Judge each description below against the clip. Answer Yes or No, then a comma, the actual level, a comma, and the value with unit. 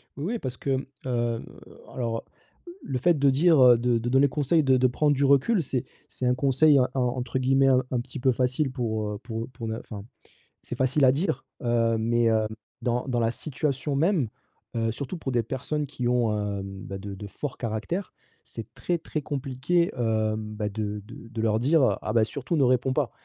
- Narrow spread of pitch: No, average, 3.4 semitones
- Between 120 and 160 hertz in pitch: Yes, low, 125 Hz